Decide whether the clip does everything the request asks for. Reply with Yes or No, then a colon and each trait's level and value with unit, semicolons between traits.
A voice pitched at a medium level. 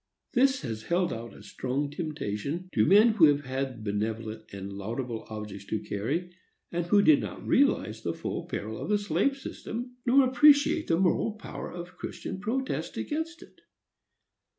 Yes: medium, 160 Hz